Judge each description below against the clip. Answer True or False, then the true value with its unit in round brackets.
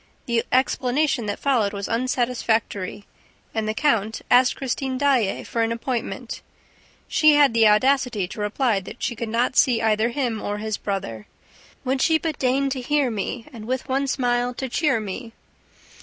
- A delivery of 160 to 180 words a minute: True (170 wpm)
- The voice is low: False (240 Hz)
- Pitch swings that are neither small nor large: True (3.3 semitones)